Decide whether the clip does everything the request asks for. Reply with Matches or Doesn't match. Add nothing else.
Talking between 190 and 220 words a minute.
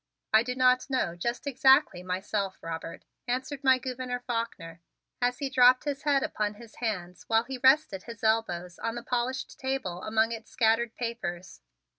Doesn't match